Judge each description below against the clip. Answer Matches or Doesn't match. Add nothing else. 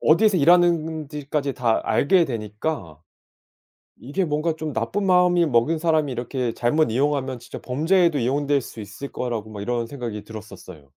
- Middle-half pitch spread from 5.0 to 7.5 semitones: Matches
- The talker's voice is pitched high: Doesn't match